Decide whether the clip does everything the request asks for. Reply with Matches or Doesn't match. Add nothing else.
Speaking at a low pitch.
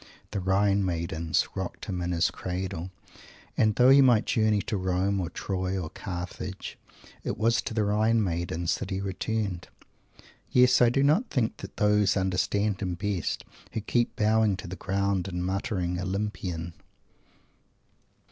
Matches